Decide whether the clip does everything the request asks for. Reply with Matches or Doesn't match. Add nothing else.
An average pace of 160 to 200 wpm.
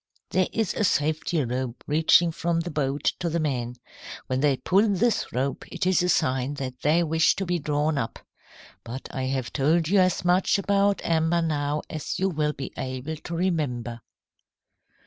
Matches